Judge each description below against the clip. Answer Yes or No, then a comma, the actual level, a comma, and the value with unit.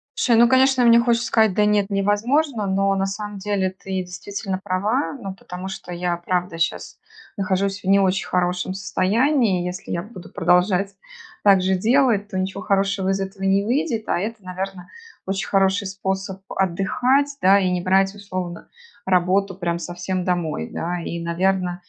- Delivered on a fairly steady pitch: Yes, narrow, 2.1 semitones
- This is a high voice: Yes, high, 195 Hz